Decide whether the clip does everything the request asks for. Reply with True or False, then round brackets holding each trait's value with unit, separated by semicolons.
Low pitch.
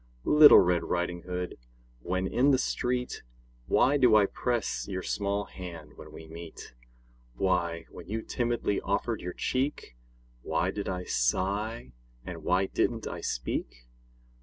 True (95 Hz)